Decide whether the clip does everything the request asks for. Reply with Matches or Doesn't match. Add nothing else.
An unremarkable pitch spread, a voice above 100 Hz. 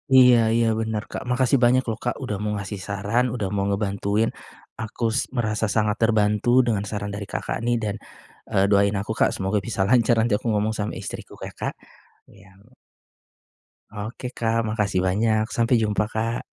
Doesn't match